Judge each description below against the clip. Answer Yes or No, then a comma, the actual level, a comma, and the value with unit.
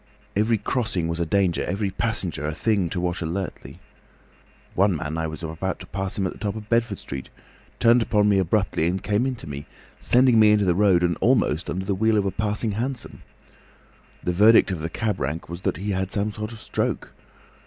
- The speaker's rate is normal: No, fast, 215 wpm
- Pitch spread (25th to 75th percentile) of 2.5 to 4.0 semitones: Yes, average, 3.7 semitones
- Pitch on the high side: No, low, 100 Hz